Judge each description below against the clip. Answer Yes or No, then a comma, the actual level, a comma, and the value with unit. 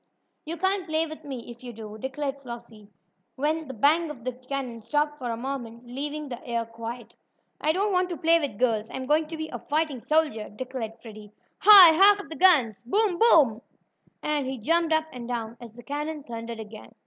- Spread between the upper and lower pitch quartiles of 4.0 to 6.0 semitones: Yes, average, 5.2 semitones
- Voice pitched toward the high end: Yes, very high, 270 Hz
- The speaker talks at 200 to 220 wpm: Yes, fast, 205 wpm